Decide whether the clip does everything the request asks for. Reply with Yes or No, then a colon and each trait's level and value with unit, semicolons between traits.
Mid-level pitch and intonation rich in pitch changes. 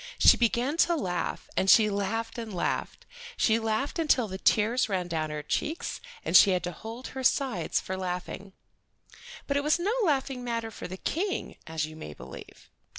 No: high, 225 Hz; wide, 6.2 semitones